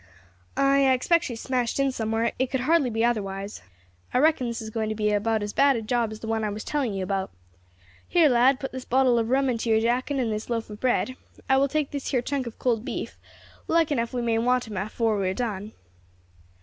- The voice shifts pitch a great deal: No, average, 3.3 semitones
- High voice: Yes, high, 235 Hz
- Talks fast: Yes, fast, 240 wpm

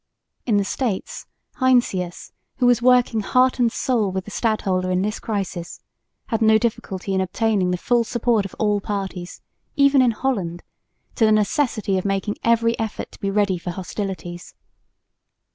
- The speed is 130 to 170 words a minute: Yes, average, 160 wpm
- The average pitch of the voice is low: No, high, 210 Hz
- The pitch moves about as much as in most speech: Yes, average, 3.7 semitones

